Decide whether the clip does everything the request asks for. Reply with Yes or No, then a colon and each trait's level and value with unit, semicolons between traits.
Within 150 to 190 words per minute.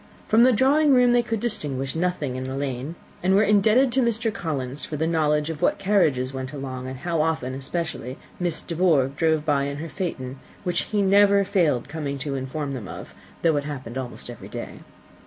No: fast, 205 wpm